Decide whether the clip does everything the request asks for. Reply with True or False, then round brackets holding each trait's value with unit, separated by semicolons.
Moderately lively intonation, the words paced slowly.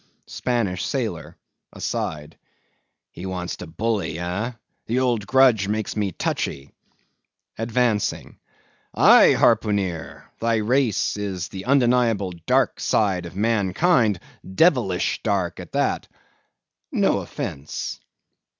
True (4.3 semitones; 95 wpm)